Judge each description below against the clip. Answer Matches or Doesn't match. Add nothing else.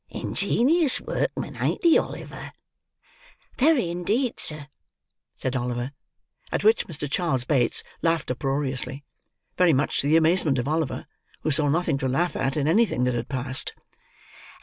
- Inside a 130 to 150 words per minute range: Matches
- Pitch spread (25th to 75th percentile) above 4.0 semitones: Matches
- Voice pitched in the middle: Matches